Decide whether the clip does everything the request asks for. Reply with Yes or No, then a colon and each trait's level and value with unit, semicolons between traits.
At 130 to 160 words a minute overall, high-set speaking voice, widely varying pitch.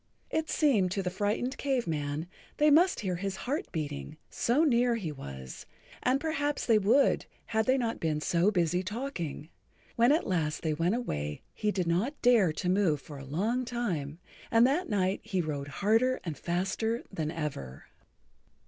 No: average, 175 wpm; high, 195 Hz; wide, 7.5 semitones